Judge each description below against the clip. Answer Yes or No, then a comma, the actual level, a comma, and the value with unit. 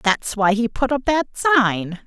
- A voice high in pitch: Yes, high, 235 Hz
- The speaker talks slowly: No, fast, 205 wpm